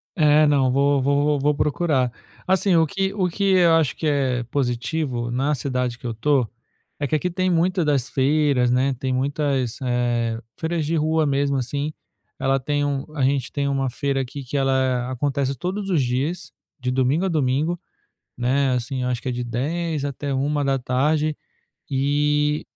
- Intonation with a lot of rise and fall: No, average, 2.9 semitones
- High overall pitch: No, medium, 140 Hz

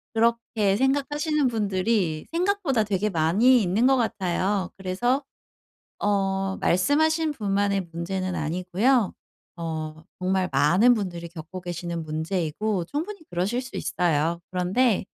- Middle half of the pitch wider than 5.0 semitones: Yes, wide, 5.6 semitones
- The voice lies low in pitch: No, high, 195 Hz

